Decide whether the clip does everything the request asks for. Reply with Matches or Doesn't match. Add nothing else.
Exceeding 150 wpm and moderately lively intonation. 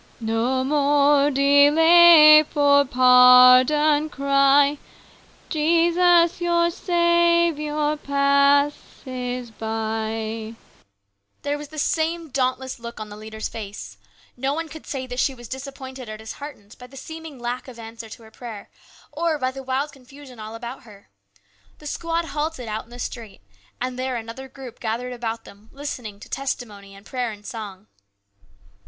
Doesn't match